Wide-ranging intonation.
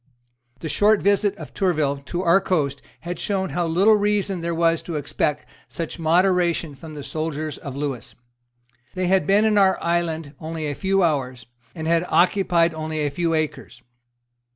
No: average, 3.6 semitones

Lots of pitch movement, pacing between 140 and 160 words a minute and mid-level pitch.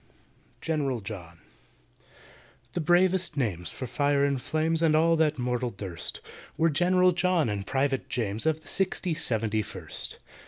Yes: wide, 6.5 semitones; average, 145 wpm; medium, 145 Hz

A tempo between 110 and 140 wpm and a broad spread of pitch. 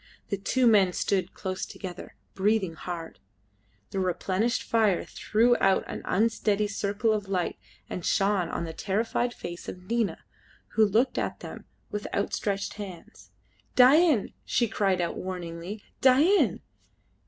No: slow, 135 wpm; average, 3.3 semitones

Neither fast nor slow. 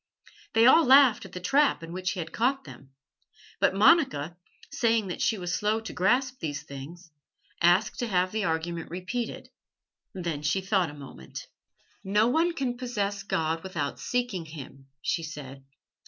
Yes: average, 165 wpm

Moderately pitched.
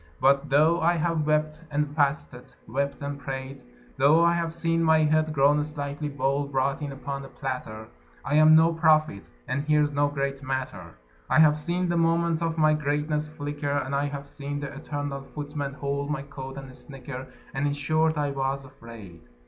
Yes: medium, 145 Hz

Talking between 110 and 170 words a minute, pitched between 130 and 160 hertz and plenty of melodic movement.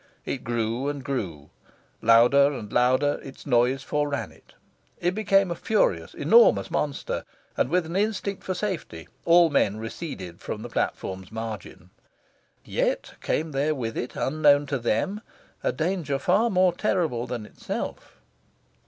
Yes: average, 145 wpm; medium, 140 Hz; wide, 7.2 semitones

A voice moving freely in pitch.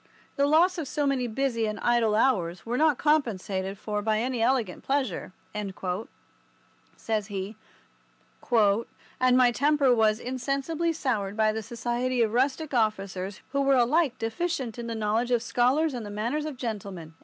No: average, 4.2 semitones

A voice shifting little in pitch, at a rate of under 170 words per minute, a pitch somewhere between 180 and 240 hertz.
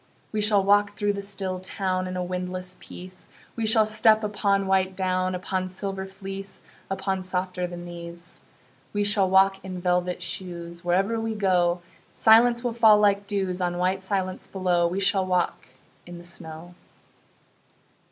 Yes: narrow, 1.9 semitones; average, 160 wpm; high, 190 Hz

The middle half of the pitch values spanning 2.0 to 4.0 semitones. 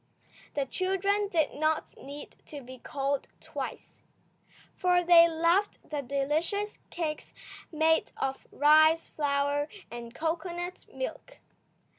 Yes: average, 3.7 semitones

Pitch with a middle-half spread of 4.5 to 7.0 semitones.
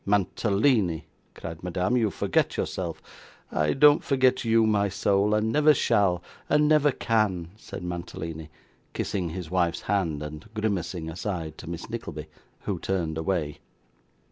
Yes: average, 5.0 semitones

